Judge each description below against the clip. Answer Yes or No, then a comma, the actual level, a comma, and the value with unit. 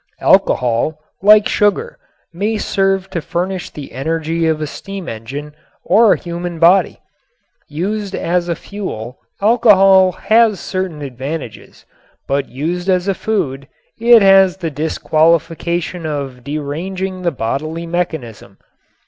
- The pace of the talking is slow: Yes, slow, 125 wpm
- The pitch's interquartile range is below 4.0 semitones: No, average, 4.4 semitones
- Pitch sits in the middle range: Yes, medium, 170 Hz